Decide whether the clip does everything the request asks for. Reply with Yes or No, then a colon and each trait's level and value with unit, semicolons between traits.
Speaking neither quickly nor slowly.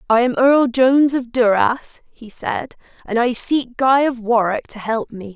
Yes: average, 190 wpm